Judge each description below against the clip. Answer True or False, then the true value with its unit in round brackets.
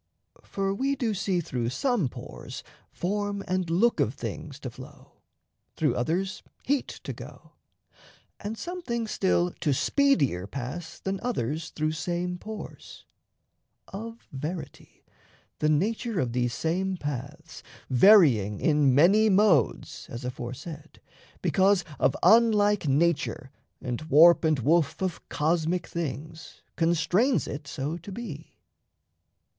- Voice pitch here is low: False (170 Hz)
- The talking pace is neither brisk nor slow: False (125 wpm)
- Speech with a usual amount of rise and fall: False (5.8 semitones)